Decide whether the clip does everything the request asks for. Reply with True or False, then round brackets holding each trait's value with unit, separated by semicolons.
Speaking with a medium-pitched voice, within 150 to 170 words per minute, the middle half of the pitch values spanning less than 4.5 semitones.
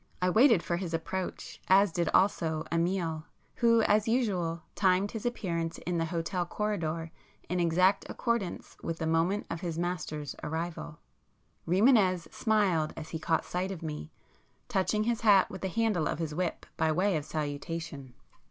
True (175 Hz; 160 wpm; 3.4 semitones)